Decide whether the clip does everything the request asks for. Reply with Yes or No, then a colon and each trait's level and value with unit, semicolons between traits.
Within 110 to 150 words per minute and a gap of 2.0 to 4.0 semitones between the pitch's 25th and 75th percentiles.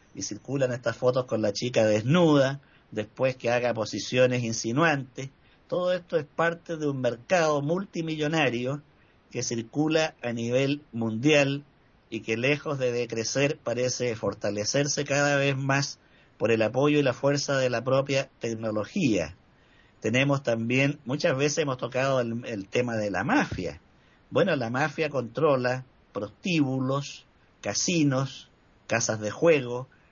Yes: average, 135 wpm; average, 3.6 semitones